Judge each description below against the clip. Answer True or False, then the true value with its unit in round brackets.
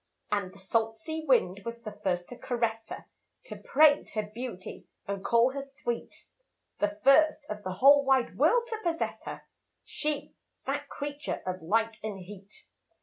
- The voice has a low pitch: False (230 Hz)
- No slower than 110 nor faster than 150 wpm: False (165 wpm)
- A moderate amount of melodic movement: False (5.7 semitones)